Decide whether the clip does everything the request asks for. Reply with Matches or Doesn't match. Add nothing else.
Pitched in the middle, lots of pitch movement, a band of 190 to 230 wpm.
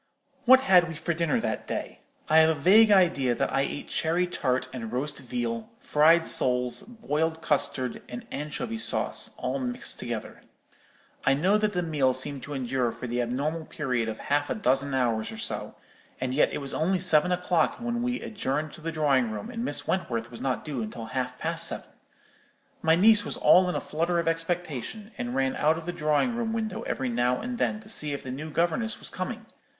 Matches